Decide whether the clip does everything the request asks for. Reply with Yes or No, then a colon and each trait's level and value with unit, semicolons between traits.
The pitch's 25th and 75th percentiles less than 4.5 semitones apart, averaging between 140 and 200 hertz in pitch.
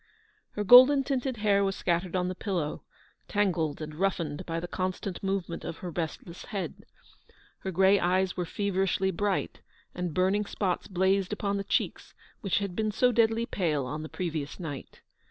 Yes: average, 2.9 semitones; high, 190 Hz